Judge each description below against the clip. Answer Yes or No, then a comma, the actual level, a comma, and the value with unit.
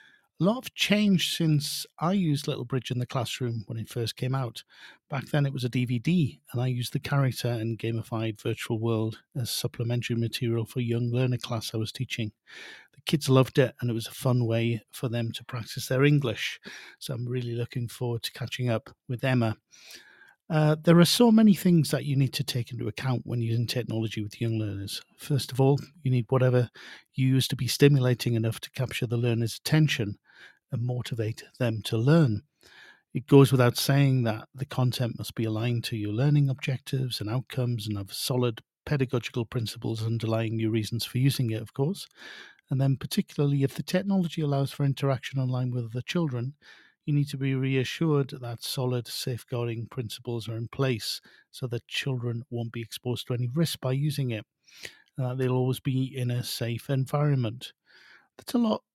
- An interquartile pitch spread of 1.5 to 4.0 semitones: Yes, average, 3.0 semitones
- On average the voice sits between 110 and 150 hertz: Yes, low, 125 Hz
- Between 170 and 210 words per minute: Yes, average, 190 wpm